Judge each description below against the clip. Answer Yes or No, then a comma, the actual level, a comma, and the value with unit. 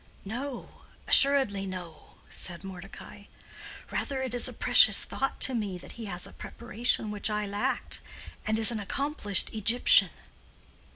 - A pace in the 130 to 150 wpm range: Yes, average, 140 wpm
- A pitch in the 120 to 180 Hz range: No, high, 215 Hz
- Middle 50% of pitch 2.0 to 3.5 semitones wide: No, average, 3.9 semitones